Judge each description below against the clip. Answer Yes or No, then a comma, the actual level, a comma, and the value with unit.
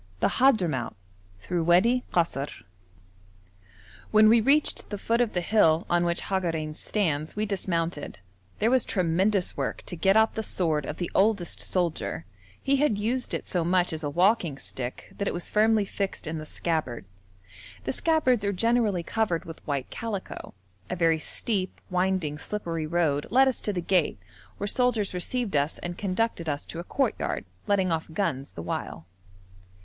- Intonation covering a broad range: No, average, 4.9 semitones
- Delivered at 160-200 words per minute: Yes, average, 170 wpm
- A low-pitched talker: No, medium, 180 Hz